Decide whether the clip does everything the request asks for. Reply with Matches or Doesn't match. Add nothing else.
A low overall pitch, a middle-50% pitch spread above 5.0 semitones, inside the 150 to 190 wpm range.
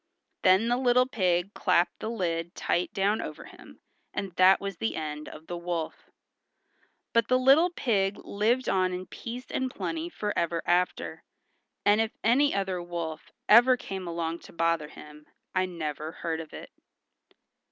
Doesn't match